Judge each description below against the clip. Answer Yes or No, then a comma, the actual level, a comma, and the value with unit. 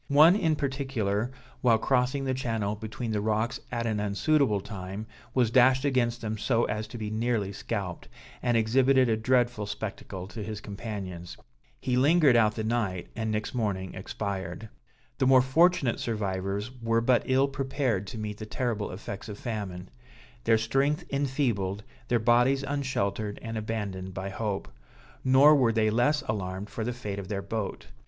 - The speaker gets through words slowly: No, average, 165 wpm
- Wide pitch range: No, average, 3.8 semitones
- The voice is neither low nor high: No, low, 115 Hz